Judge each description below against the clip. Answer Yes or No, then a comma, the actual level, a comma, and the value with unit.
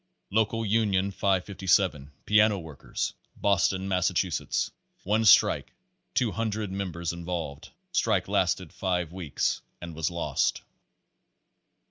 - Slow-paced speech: Yes, slow, 100 wpm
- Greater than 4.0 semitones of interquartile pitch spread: No, average, 3.3 semitones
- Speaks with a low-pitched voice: Yes, very low, 95 Hz